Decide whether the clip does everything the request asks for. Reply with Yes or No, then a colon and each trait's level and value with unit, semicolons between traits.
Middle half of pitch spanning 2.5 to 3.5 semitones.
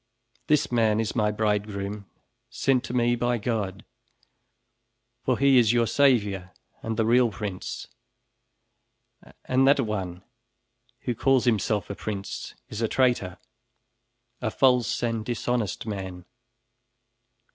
Yes: average, 3.1 semitones